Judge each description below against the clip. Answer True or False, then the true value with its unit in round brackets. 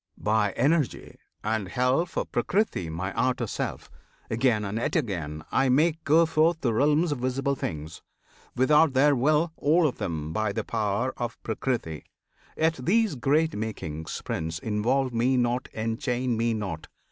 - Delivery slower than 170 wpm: True (155 wpm)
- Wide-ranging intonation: True (5.8 semitones)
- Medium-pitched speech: False (125 Hz)